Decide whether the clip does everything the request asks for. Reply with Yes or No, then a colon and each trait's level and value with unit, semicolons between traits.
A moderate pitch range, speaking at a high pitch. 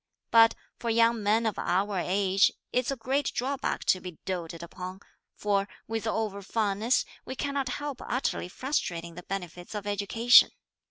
Yes: average, 4.2 semitones; high, 210 Hz